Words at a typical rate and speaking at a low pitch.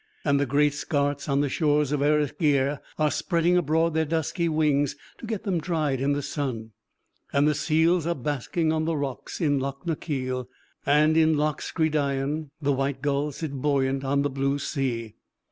No: average, 180 wpm; medium, 145 Hz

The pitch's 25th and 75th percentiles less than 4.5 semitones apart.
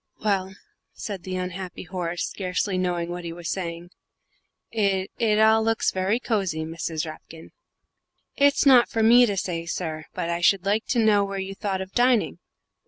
Yes: average, 3.6 semitones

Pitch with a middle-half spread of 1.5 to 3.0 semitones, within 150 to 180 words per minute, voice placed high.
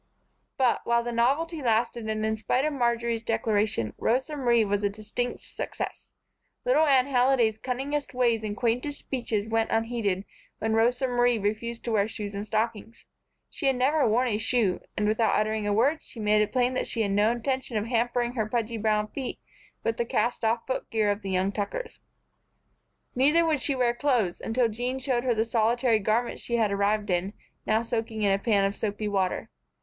No: average, 2.7 semitones; average, 190 wpm; high, 230 Hz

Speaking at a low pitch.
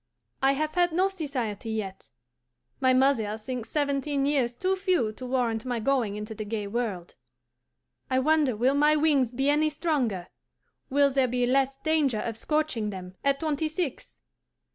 No: very high, 265 Hz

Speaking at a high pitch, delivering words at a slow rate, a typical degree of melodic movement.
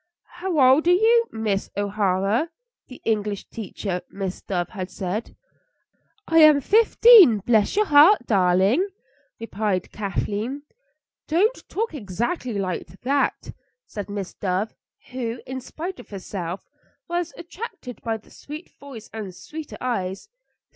No: high, 230 Hz; slow, 125 wpm; wide, 7.7 semitones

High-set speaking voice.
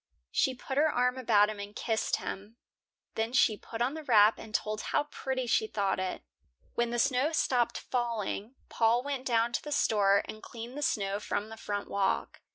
Yes: high, 230 Hz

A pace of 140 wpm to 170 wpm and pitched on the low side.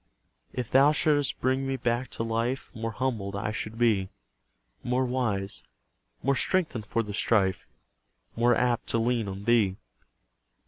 Yes: average, 145 wpm; low, 120 Hz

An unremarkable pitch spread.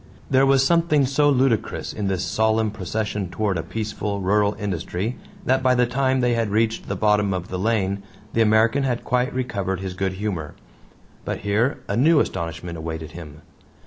Yes: average, 4.7 semitones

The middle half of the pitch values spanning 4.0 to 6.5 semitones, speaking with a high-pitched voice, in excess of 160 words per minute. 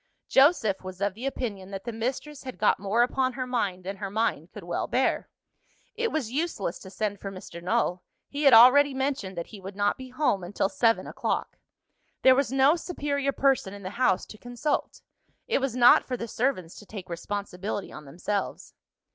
Yes: wide, 5.4 semitones; high, 225 Hz; average, 195 wpm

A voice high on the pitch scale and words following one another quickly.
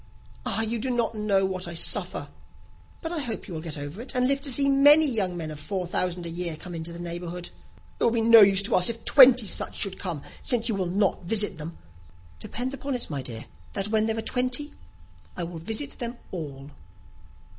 Yes: high, 200 Hz; fast, 220 wpm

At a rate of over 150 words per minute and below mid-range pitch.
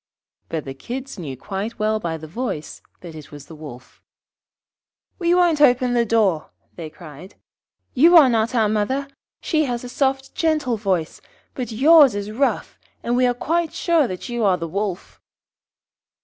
No: average, 170 wpm; high, 225 Hz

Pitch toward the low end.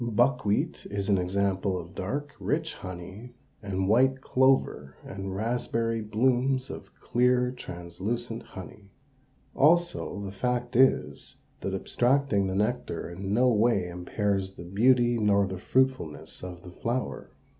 Yes: low, 105 Hz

